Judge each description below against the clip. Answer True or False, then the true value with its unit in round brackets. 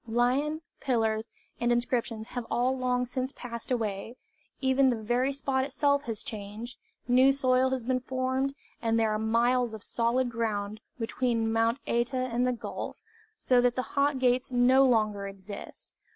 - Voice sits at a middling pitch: False (245 Hz)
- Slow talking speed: False (160 wpm)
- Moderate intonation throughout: False (2.3 semitones)